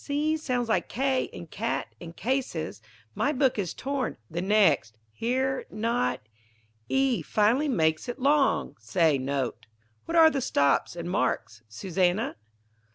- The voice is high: Yes, high, 225 Hz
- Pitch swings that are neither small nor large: No, wide, 8.3 semitones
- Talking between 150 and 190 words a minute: No, average, 140 wpm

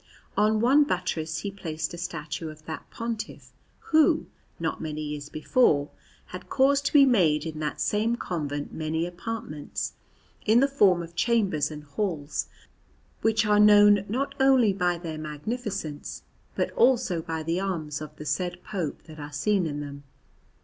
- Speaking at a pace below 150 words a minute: No, average, 160 wpm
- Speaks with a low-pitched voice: No, medium, 175 Hz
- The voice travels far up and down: Yes, wide, 5.9 semitones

